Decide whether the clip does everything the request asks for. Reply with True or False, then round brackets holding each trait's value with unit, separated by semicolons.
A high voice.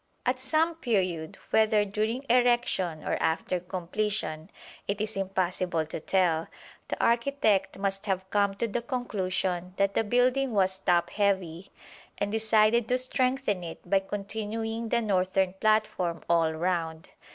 True (200 Hz)